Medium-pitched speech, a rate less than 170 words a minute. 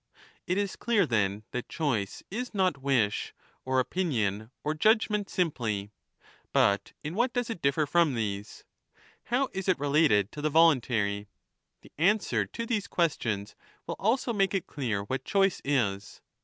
Yes: medium, 150 Hz; average, 155 wpm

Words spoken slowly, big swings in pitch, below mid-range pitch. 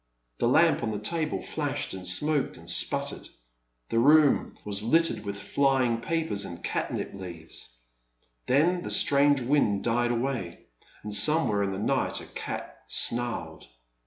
No: average, 145 wpm; wide, 6.2 semitones; low, 120 Hz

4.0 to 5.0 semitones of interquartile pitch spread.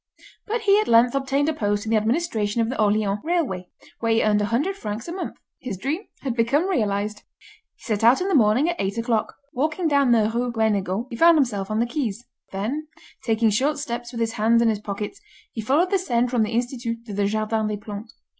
Yes: average, 4.7 semitones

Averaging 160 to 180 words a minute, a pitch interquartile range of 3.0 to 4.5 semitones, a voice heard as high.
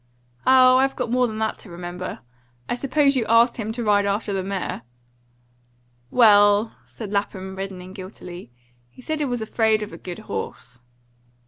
Yes: average, 165 wpm; average, 4.1 semitones; high, 210 Hz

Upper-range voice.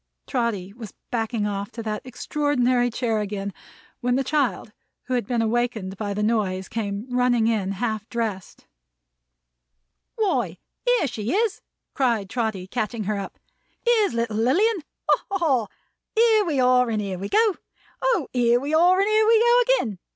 Yes: high, 240 Hz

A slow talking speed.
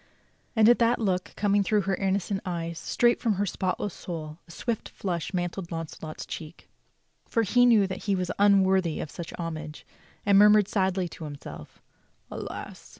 No: average, 175 wpm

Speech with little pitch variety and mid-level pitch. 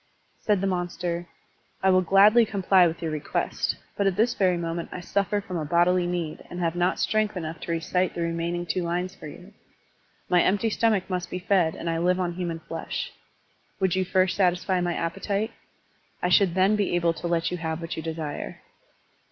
Yes: narrow, 2.2 semitones; medium, 180 Hz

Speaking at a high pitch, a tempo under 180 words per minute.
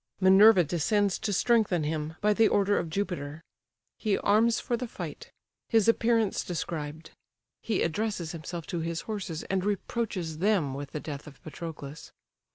No: medium, 180 Hz; average, 155 wpm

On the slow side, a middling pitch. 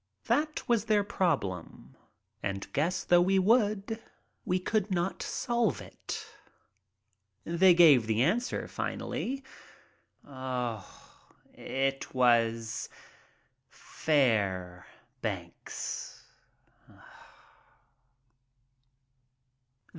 Yes: slow, 65 wpm; medium, 175 Hz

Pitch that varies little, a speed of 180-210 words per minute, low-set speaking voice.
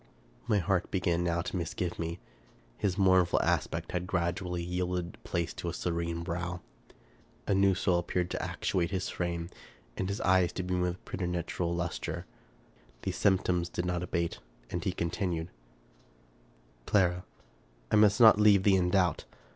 No: narrow, 1.5 semitones; average, 160 wpm; very low, 90 Hz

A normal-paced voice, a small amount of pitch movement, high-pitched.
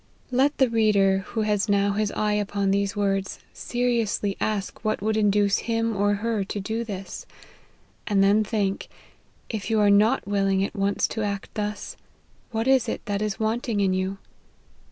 Yes: average, 175 wpm; narrow, 1.9 semitones; high, 205 Hz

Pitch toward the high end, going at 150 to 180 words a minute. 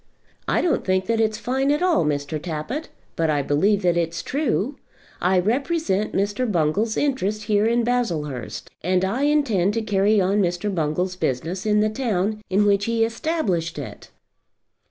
Yes: high, 205 Hz; average, 165 wpm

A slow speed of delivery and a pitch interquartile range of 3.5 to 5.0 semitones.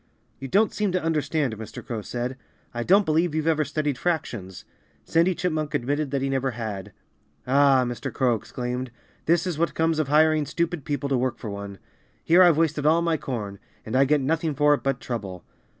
No: average, 195 wpm; average, 4.5 semitones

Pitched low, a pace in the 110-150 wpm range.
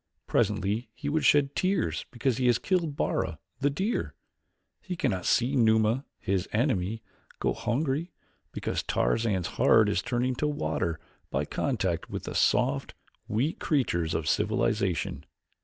Yes: low, 120 Hz; average, 140 wpm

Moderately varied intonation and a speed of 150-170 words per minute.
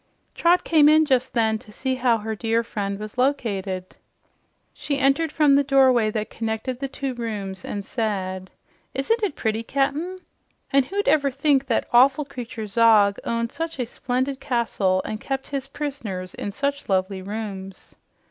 Yes: average, 4.7 semitones; average, 165 wpm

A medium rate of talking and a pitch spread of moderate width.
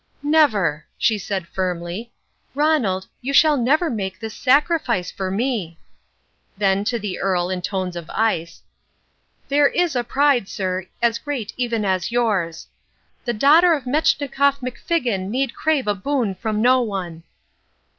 No: average, 145 wpm; wide, 6.6 semitones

